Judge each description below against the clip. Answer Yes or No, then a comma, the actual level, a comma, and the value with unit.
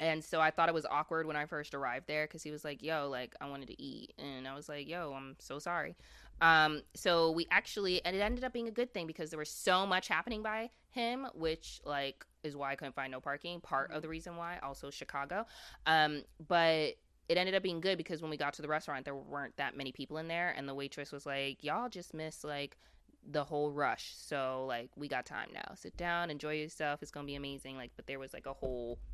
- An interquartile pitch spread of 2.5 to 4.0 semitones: Yes, average, 3.6 semitones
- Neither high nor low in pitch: Yes, medium, 155 Hz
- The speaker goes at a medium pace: No, fast, 250 wpm